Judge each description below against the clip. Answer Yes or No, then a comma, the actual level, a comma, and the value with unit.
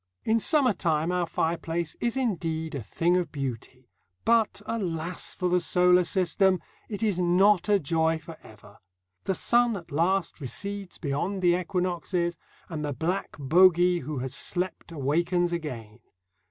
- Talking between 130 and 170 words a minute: Yes, average, 150 wpm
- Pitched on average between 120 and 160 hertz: No, medium, 175 Hz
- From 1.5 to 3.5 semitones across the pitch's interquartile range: Yes, average, 3.0 semitones